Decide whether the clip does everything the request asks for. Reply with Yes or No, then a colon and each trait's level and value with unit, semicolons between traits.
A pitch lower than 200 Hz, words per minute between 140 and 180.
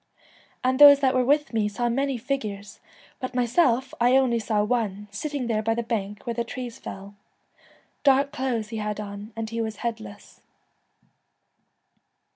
No: high, 235 Hz; average, 160 wpm